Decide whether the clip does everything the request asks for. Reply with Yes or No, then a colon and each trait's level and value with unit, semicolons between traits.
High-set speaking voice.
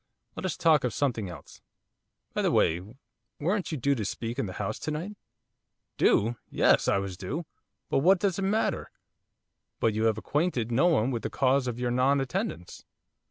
No: low, 130 Hz